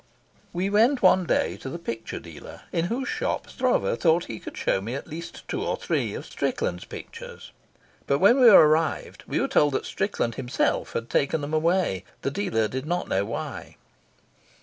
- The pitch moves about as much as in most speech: No, wide, 6.6 semitones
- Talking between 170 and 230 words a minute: Yes, average, 180 wpm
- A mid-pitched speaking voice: Yes, medium, 160 Hz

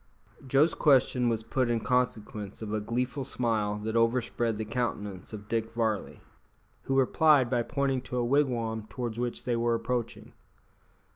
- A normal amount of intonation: No, narrow, 2.2 semitones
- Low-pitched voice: Yes, low, 120 Hz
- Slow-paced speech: No, average, 155 wpm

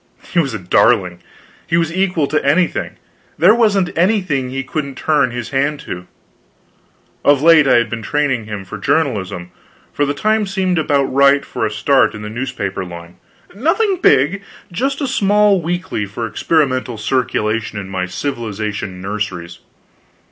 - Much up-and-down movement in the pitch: Yes, wide, 8.0 semitones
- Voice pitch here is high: No, low, 135 Hz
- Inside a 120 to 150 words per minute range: No, average, 160 wpm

